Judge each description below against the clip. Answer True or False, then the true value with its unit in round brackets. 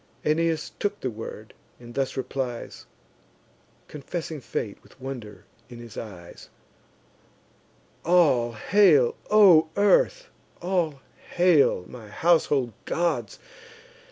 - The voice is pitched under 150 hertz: True (140 Hz)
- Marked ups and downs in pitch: True (6.6 semitones)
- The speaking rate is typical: False (100 wpm)